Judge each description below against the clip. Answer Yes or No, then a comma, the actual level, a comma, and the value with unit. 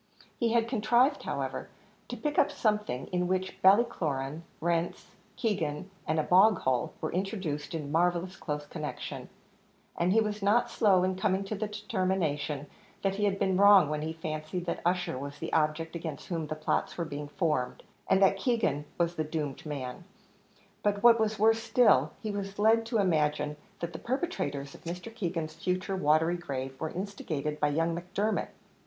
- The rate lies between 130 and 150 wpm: No, average, 175 wpm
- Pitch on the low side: No, medium, 180 Hz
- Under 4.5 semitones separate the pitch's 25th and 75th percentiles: No, average, 5.0 semitones